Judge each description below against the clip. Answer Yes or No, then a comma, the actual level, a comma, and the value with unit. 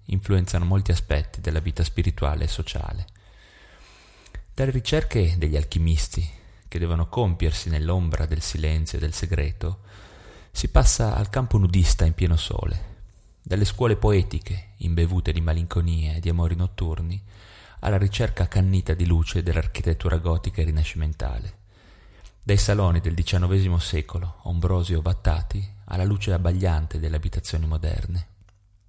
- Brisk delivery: No, average, 130 wpm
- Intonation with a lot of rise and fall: No, average, 2.9 semitones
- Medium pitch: No, very low, 90 Hz